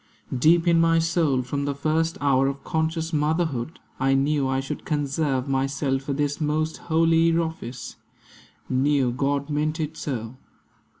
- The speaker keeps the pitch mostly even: No, average, 3.0 semitones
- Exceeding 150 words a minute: No, average, 145 wpm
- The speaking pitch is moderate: Yes, medium, 145 Hz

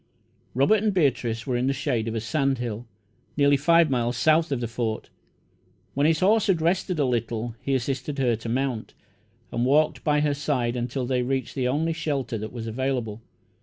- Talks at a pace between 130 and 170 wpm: No, average, 195 wpm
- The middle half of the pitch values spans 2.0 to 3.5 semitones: No, average, 3.9 semitones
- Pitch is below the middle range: Yes, low, 130 Hz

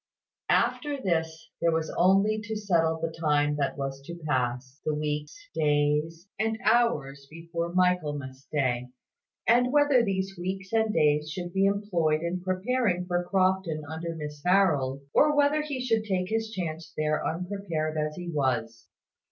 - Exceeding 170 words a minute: No, average, 150 wpm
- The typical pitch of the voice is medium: Yes, medium, 170 Hz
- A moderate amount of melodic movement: Yes, average, 4.7 semitones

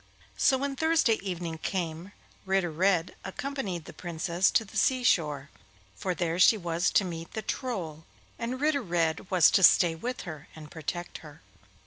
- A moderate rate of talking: Yes, average, 165 wpm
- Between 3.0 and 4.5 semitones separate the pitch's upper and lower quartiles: No, average, 5.1 semitones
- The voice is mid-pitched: Yes, medium, 180 Hz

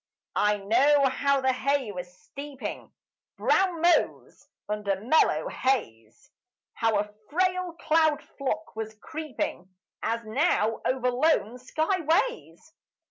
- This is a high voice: Yes, very high, 265 Hz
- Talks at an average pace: No, slow, 115 wpm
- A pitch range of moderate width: No, wide, 6.4 semitones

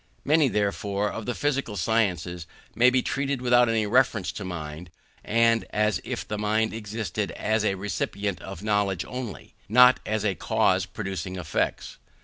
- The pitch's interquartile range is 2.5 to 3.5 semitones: Yes, average, 3.1 semitones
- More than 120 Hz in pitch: No, low, 105 Hz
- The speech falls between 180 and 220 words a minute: No, average, 160 wpm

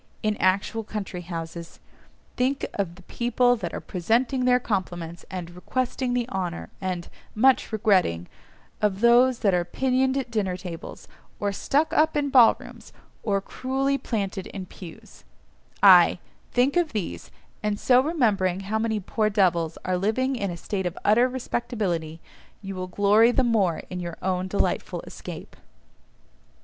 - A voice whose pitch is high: Yes, high, 205 Hz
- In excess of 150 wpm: No, average, 145 wpm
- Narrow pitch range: No, average, 5.3 semitones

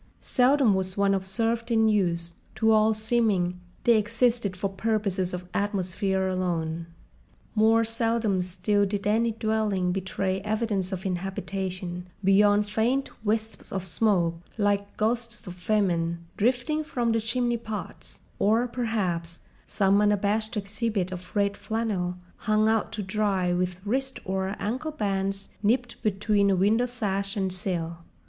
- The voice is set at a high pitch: Yes, high, 205 Hz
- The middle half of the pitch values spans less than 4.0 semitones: Yes, average, 3.0 semitones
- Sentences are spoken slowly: Yes, slow, 130 wpm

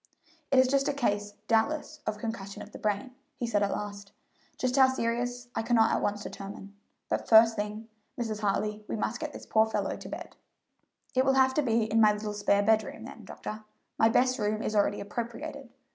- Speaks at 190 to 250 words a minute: Yes, average, 200 wpm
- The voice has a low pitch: No, high, 220 Hz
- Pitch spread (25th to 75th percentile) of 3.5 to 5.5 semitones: No, average, 3.0 semitones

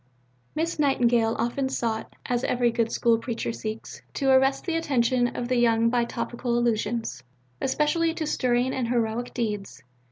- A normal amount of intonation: No, narrow, 2.3 semitones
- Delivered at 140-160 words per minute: Yes, average, 155 wpm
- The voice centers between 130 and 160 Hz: No, high, 240 Hz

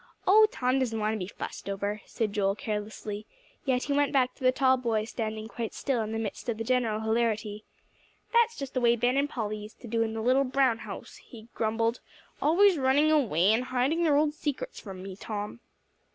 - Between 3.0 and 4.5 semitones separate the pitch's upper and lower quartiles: Yes, average, 3.8 semitones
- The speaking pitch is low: No, high, 235 Hz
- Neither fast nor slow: No, fast, 210 wpm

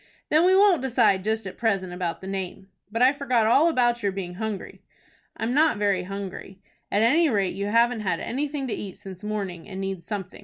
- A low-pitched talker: No, high, 210 Hz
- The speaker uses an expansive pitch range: No, average, 4.3 semitones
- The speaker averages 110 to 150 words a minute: No, fast, 205 wpm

